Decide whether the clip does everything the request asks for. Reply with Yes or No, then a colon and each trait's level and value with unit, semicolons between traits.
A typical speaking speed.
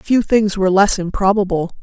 Yes: average, 165 wpm